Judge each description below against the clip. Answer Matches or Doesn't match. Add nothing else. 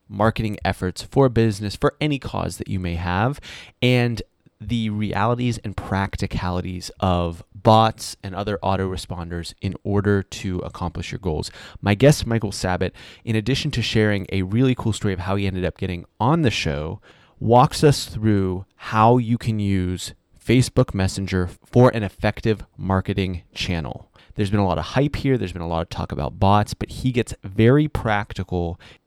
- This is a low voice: Matches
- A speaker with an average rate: Matches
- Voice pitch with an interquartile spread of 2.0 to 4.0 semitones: Matches